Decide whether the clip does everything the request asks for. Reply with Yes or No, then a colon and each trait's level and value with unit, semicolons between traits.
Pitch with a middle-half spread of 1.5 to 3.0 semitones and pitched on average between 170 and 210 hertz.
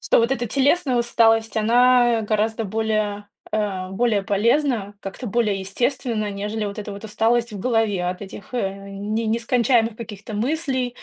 No: average, 2.7 semitones; high, 220 Hz